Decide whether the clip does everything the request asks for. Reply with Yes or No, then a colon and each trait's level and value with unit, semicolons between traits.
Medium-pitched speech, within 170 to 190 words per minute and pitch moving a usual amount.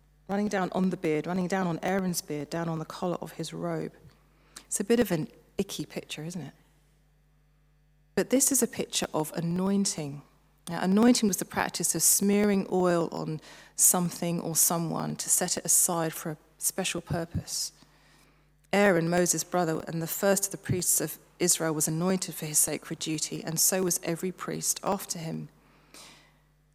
Yes: medium, 170 Hz; average, 175 wpm; average, 3.2 semitones